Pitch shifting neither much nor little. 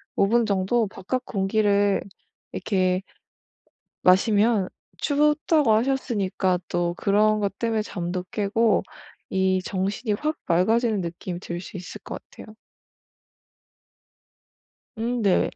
Yes: average, 3.4 semitones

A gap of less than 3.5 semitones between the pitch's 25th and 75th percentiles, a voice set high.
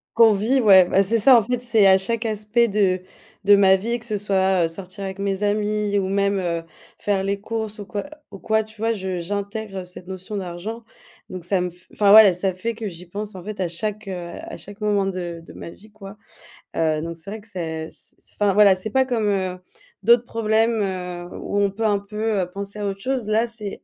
Yes: narrow, 2.5 semitones; high, 200 Hz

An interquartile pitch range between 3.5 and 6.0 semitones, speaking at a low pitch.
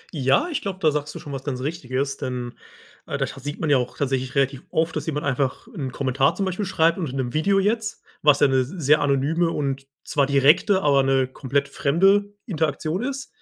No: average, 3.9 semitones; medium, 145 Hz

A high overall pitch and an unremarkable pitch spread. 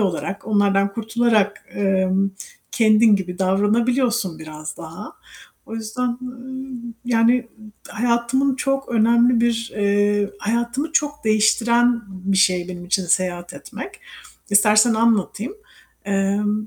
Yes: high, 215 Hz; average, 3.3 semitones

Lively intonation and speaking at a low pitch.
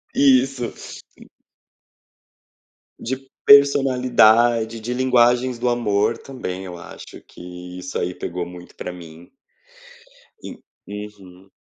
Yes: wide, 5.7 semitones; low, 115 Hz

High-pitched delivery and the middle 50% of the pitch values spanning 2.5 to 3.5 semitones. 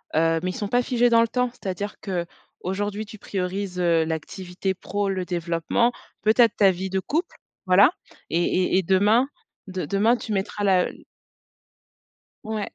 Yes: high, 195 Hz; average, 3.0 semitones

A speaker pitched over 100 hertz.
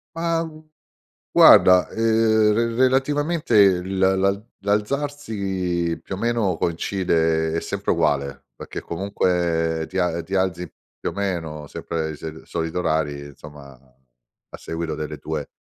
No: very low, 90 Hz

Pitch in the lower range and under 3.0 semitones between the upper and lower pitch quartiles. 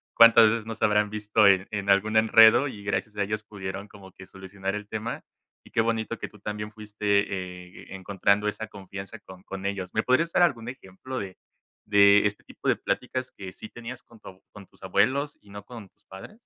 Yes: low, 105 Hz; narrow, 2.4 semitones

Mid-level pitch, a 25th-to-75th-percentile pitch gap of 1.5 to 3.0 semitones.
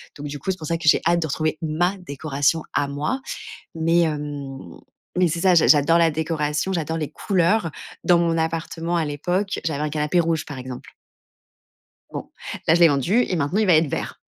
Yes: medium, 160 Hz; narrow, 2.6 semitones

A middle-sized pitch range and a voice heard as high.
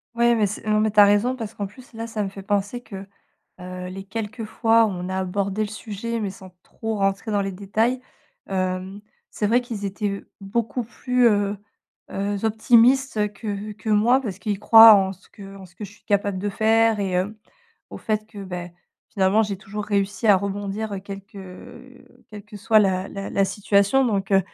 No: narrow, 2.2 semitones; high, 205 Hz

